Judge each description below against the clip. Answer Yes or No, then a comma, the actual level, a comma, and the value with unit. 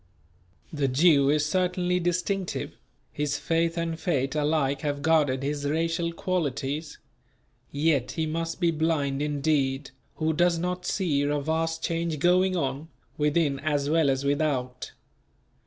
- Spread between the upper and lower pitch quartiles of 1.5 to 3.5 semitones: Yes, average, 2.8 semitones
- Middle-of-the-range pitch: Yes, medium, 155 Hz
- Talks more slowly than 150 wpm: Yes, slow, 135 wpm